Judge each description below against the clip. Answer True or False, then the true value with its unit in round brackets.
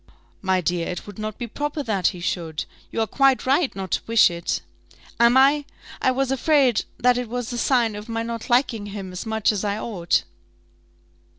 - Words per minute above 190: True (200 wpm)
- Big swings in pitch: False (4.5 semitones)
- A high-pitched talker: True (225 Hz)